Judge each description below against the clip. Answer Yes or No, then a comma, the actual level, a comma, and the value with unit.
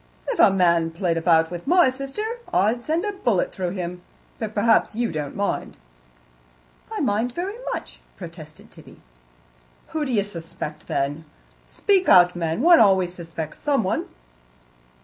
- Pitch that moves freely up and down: Yes, wide, 7.2 semitones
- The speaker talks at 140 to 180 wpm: Yes, average, 145 wpm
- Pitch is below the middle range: No, high, 190 Hz